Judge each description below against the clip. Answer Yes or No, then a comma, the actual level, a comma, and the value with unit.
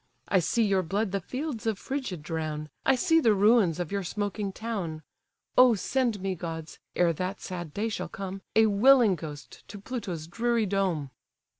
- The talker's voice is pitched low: No, high, 195 Hz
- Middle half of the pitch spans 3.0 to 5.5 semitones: Yes, average, 4.7 semitones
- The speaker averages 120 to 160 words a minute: No, average, 175 wpm